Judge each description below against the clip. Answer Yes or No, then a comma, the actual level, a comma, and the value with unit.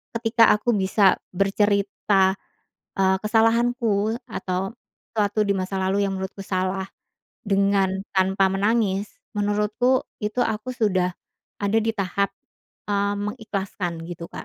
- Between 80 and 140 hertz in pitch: No, high, 200 Hz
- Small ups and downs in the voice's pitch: Yes, narrow, 2.1 semitones